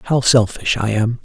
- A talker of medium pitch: No, low, 115 Hz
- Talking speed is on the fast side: No, average, 195 wpm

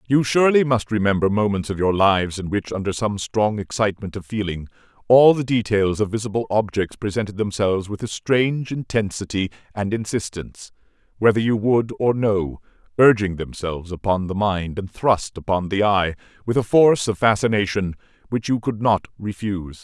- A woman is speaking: No, male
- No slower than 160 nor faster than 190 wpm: Yes, average, 165 wpm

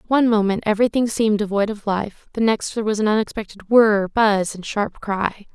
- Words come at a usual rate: Yes, average, 195 wpm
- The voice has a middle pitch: No, high, 210 Hz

